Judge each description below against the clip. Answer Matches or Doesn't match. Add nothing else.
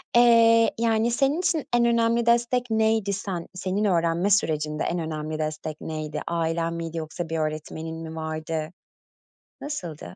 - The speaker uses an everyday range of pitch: Doesn't match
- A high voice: Doesn't match